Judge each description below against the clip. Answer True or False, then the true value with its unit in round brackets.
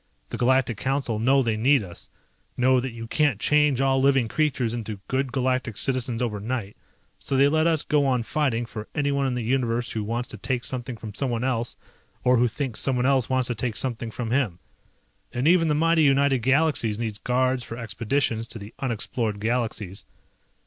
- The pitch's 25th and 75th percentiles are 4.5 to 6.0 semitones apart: False (2.9 semitones)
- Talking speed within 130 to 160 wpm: False (190 wpm)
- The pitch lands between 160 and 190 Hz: False (125 Hz)